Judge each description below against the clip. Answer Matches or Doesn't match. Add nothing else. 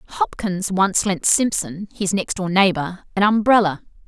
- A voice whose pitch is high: Matches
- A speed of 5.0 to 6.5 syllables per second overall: Doesn't match